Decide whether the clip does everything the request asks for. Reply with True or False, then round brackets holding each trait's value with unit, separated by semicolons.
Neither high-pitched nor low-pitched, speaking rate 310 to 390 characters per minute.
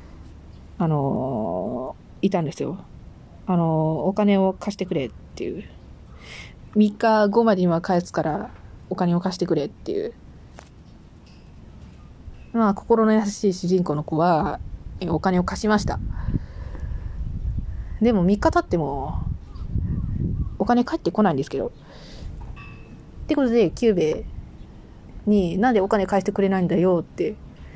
False (180 Hz; 240 characters per minute)